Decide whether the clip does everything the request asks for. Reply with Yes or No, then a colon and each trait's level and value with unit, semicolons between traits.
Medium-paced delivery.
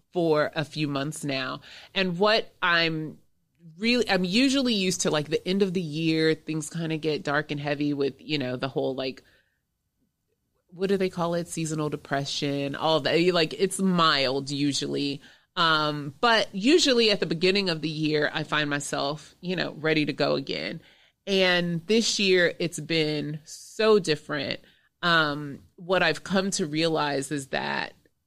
Yes: average, 165 wpm